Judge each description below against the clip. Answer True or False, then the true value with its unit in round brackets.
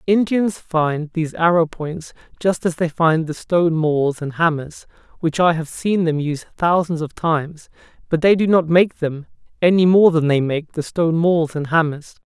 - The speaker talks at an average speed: True (190 wpm)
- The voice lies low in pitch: False (165 Hz)